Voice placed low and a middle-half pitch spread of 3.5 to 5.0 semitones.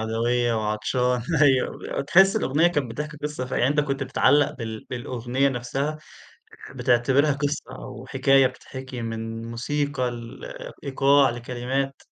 No: low, 130 Hz; average, 3.1 semitones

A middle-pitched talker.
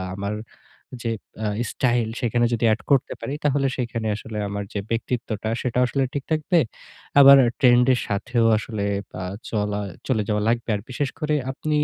No: low, 120 Hz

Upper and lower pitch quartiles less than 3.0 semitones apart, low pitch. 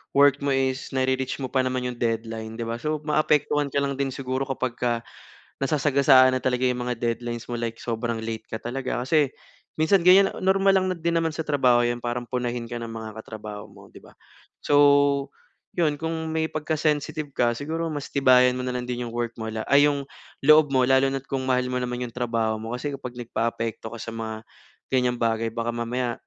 No: average, 3.3 semitones; low, 130 Hz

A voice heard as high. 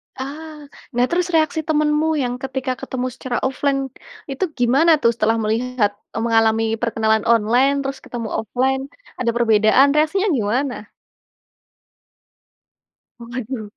Yes: very high, 250 Hz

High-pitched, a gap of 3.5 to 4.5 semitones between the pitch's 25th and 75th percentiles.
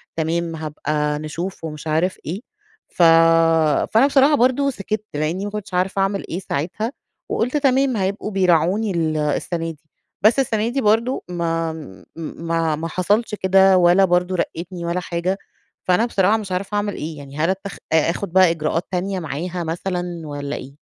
No: medium, 180 Hz; average, 3.8 semitones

